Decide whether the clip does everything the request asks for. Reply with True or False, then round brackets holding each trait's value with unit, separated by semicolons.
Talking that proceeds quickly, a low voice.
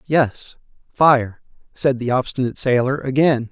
False (120 wpm; 130 Hz)